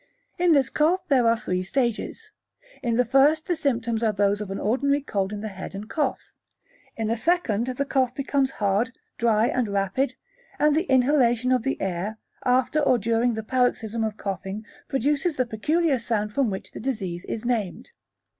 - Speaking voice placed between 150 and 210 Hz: No, high, 240 Hz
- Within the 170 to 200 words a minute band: Yes, average, 185 wpm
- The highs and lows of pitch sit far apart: No, average, 4.3 semitones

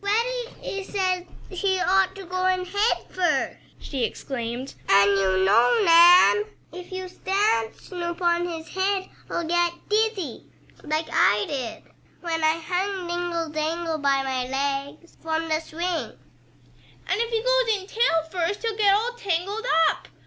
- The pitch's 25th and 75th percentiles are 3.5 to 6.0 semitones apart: Yes, average, 4.0 semitones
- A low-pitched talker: No, very high, 350 Hz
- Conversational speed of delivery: Yes, average, 150 wpm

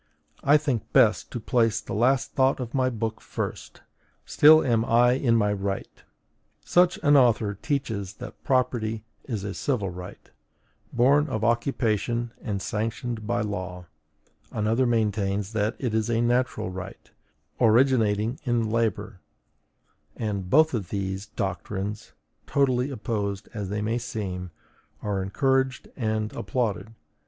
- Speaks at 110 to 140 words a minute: Yes, slow, 135 wpm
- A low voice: Yes, low, 115 Hz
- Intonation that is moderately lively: Yes, average, 3.4 semitones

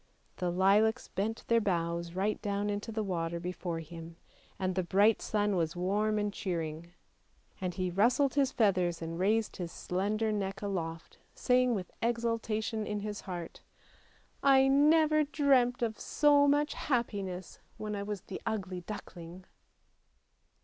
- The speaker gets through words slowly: No, average, 150 wpm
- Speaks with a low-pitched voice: No, high, 205 Hz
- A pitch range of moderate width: Yes, average, 4.0 semitones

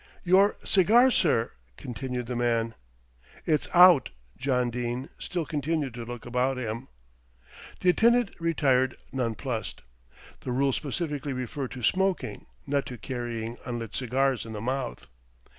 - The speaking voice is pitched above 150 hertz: No, low, 130 Hz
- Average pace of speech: No, slow, 130 wpm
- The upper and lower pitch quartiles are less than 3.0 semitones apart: No, average, 4.3 semitones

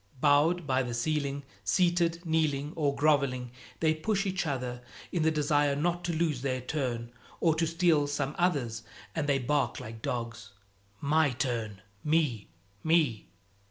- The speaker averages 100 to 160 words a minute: Yes, average, 150 wpm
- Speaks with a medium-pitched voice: Yes, medium, 145 Hz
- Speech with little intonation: No, average, 4.1 semitones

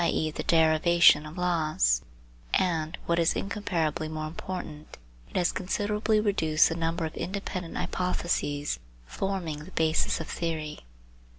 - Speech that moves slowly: Yes, slow, 130 wpm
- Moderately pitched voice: Yes, medium, 165 Hz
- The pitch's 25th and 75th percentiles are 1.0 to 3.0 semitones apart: Yes, average, 2.7 semitones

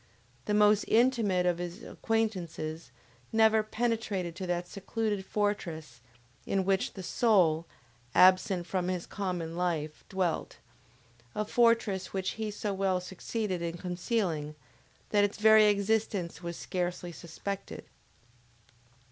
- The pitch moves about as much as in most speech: Yes, average, 3.3 semitones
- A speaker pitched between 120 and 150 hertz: No, high, 190 Hz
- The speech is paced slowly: Yes, slow, 120 wpm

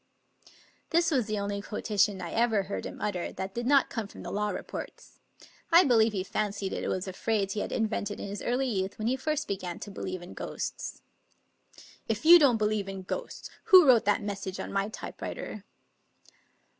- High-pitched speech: Yes, high, 210 Hz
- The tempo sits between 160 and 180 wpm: No, fast, 205 wpm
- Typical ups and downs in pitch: Yes, average, 3.5 semitones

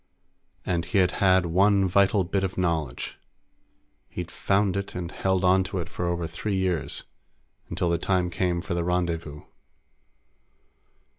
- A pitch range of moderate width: No, narrow, 1.9 semitones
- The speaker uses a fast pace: No, average, 150 wpm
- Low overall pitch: Yes, very low, 90 Hz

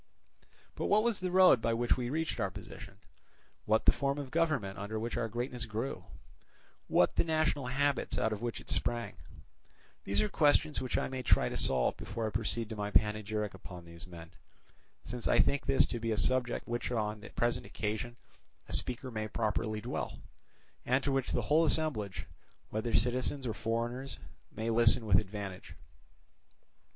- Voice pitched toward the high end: No, low, 115 Hz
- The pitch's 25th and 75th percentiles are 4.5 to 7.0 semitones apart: No, average, 3.8 semitones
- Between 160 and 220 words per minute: Yes, average, 180 wpm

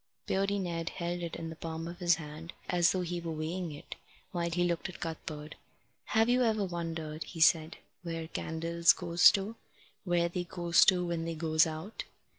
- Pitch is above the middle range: No, medium, 170 Hz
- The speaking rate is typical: Yes, average, 190 wpm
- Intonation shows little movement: Yes, narrow, 1.6 semitones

